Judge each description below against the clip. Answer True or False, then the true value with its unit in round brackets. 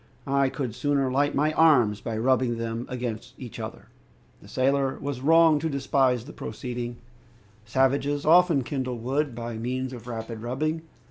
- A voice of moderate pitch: False (130 Hz)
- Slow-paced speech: False (155 wpm)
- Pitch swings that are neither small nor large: True (3.1 semitones)